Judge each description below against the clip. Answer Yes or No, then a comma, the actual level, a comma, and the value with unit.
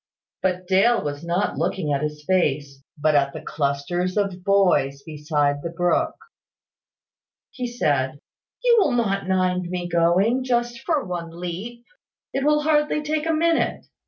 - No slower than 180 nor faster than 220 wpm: No, average, 150 wpm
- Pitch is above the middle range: No, medium, 180 Hz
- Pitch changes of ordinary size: No, wide, 7.9 semitones